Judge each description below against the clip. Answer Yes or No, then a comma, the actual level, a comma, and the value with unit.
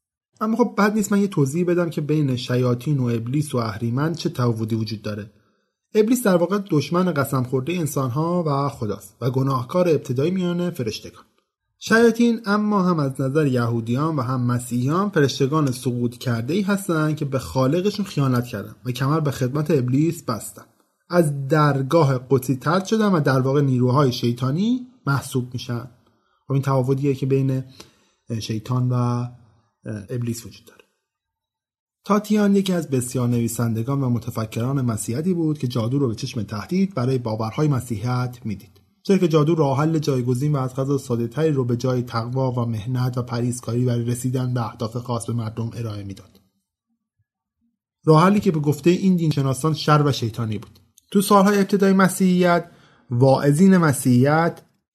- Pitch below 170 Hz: Yes, low, 135 Hz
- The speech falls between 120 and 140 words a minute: No, fast, 155 wpm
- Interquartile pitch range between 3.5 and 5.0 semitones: No, wide, 5.5 semitones